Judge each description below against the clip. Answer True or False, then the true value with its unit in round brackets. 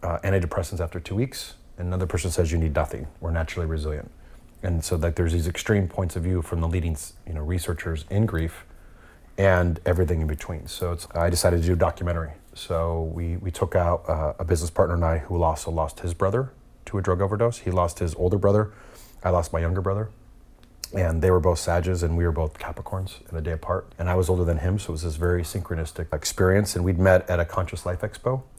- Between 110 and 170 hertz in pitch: False (90 Hz)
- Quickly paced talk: True (230 wpm)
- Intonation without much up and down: True (2.2 semitones)